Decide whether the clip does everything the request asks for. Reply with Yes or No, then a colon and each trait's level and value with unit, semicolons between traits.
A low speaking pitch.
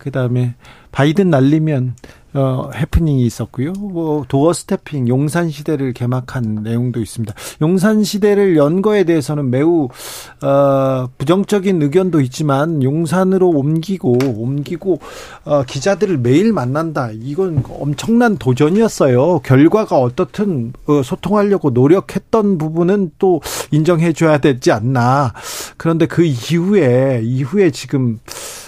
No: medium, 150 Hz